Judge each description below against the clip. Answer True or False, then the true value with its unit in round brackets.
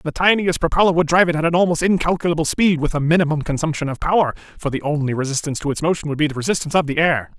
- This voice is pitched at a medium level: True (160 Hz)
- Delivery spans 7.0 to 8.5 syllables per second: True (7.4 syllables/s)